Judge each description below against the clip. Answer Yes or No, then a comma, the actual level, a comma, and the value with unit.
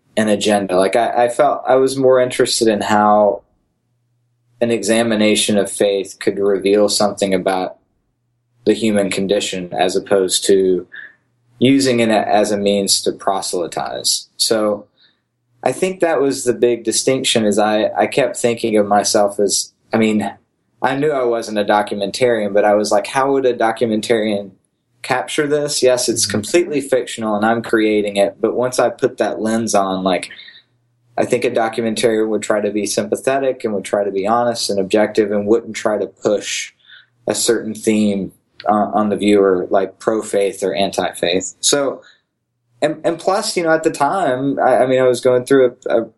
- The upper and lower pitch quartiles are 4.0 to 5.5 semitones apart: No, average, 2.9 semitones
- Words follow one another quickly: No, average, 175 wpm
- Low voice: Yes, low, 110 Hz